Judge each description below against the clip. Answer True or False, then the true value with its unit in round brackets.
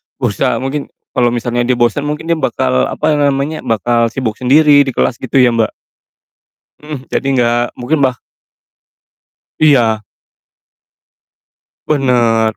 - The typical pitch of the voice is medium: False (125 Hz)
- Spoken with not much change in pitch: False (3.6 semitones)